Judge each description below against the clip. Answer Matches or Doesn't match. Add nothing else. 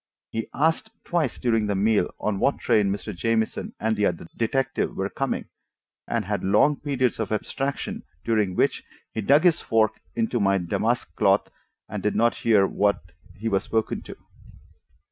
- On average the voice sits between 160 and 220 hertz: Doesn't match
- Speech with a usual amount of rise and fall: Matches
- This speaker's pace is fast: Doesn't match